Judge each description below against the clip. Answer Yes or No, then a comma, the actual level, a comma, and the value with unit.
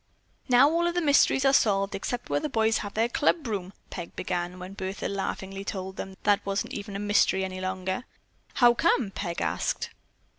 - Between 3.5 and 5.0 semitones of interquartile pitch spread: Yes, average, 4.3 semitones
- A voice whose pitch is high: Yes, high, 200 Hz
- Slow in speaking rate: No, average, 190 wpm